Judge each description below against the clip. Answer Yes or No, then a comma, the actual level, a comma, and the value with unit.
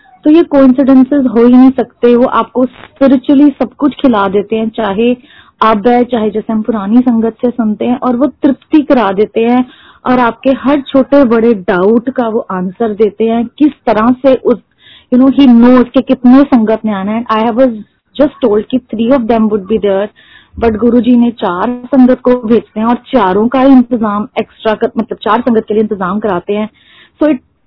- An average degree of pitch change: Yes, average, 3.0 semitones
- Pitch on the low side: No, high, 240 Hz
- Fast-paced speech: Yes, fast, 205 wpm